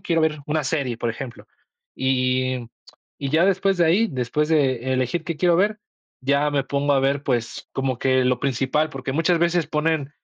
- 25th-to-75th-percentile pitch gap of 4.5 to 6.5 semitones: No, average, 3.9 semitones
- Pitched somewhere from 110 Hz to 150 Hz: Yes, medium, 140 Hz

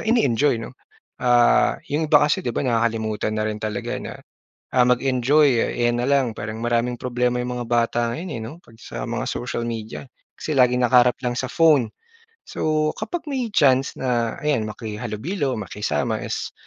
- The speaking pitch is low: Yes, low, 125 Hz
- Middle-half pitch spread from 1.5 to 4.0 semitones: Yes, average, 3.4 semitones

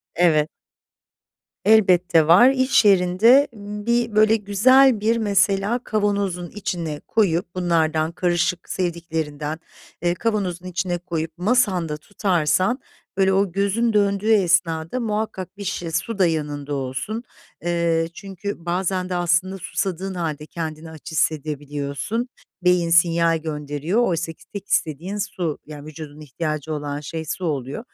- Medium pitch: Yes, medium, 175 Hz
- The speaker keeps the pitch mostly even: No, average, 4.1 semitones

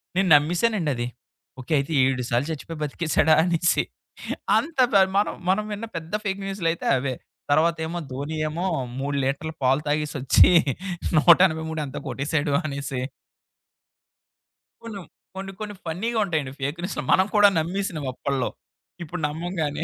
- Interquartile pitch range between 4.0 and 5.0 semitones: Yes, average, 4.6 semitones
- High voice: No, medium, 160 Hz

